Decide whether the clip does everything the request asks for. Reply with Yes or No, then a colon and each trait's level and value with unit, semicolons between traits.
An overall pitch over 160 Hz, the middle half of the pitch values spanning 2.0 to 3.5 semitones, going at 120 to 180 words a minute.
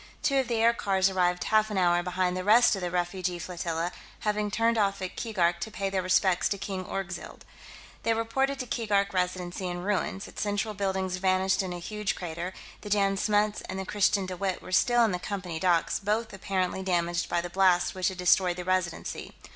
No: high, 190 Hz; narrow, 2.5 semitones; fast, 205 wpm